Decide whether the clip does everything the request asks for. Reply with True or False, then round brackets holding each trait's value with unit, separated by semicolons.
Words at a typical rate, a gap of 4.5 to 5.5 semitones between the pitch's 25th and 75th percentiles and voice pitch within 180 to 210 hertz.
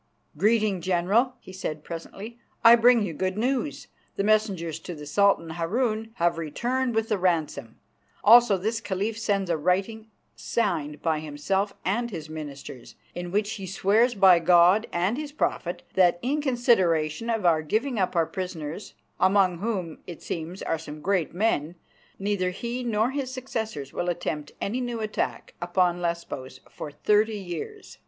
True (160 wpm; 4.9 semitones; 190 Hz)